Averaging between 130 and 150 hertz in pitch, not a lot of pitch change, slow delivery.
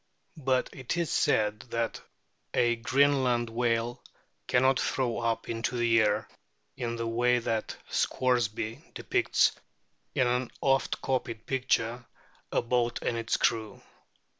No: low, 120 Hz; narrow, 1.8 semitones; slow, 125 wpm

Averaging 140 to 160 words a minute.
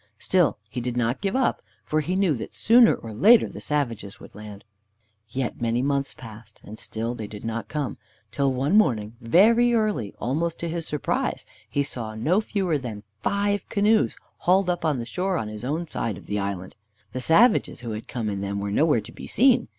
No: fast, 205 wpm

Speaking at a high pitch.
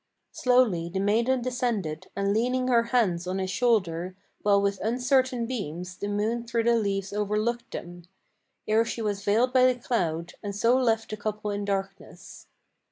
Yes: high, 215 Hz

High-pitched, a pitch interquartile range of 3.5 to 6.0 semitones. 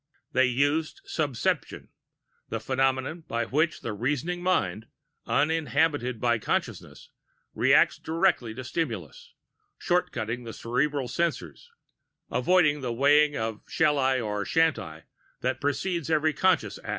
No: low, 135 Hz; average, 5.1 semitones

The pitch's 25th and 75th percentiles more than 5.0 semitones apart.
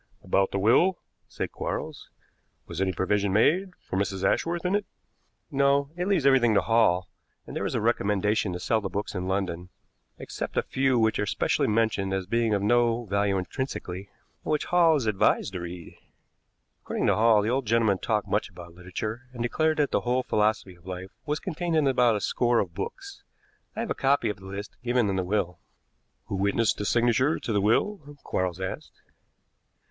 Yes: wide, 5.5 semitones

